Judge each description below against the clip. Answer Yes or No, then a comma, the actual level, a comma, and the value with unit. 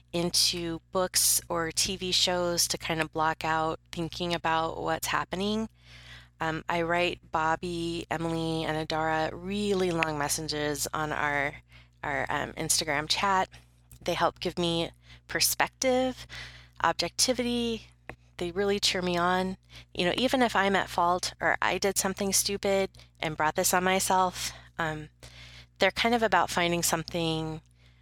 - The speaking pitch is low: No, medium, 165 Hz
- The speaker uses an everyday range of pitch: Yes, average, 3.4 semitones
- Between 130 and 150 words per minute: Yes, average, 140 wpm